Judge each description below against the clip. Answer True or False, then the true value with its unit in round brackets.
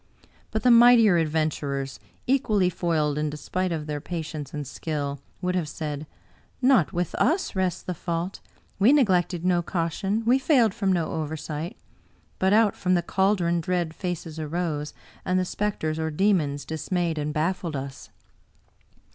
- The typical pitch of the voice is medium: True (170 Hz)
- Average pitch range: True (3.7 semitones)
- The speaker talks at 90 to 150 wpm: False (160 wpm)